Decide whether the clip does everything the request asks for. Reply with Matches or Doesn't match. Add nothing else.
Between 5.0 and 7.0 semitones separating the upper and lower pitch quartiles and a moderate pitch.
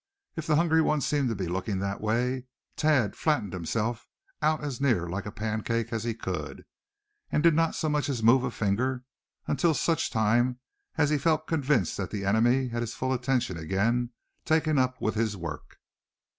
Doesn't match